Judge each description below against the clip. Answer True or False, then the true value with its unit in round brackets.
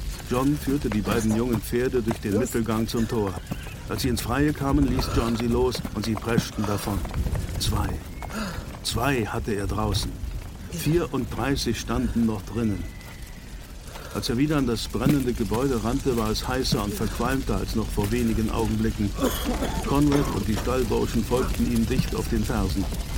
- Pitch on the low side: True (115 Hz)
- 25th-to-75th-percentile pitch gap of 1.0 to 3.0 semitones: False (3.4 semitones)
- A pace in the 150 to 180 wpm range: True (160 wpm)